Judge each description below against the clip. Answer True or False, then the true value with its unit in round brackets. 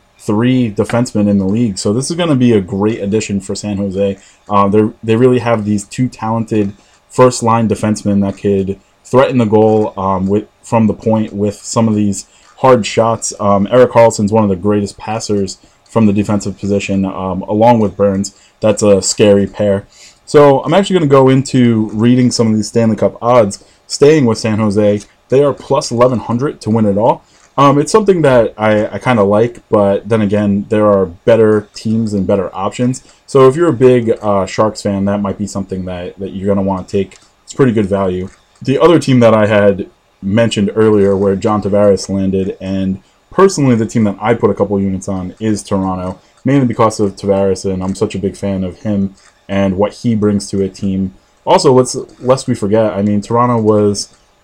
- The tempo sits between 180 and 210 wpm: True (200 wpm)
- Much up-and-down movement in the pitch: False (2.7 semitones)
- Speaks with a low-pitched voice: True (105 Hz)